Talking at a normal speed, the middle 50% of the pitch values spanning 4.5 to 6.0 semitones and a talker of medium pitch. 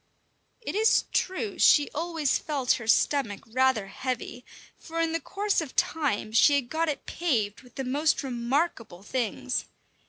No: average, 155 wpm; average, 5.3 semitones; very high, 275 Hz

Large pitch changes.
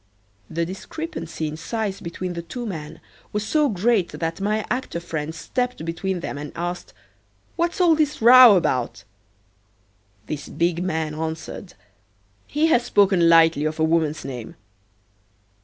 Yes: wide, 5.7 semitones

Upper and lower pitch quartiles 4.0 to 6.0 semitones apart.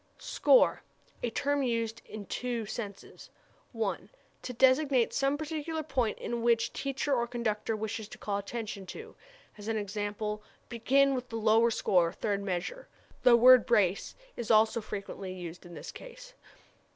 No: average, 3.6 semitones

